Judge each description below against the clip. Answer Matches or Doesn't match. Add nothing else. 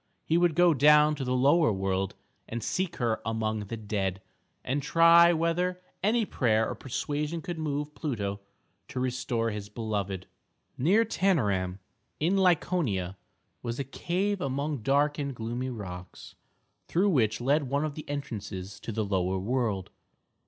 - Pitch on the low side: Matches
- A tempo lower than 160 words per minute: Matches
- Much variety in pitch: Matches